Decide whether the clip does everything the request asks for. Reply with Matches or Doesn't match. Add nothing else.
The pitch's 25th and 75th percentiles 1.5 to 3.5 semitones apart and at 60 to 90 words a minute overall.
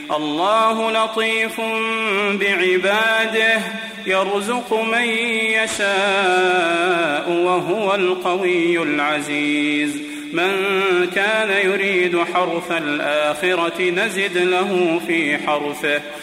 Doesn't match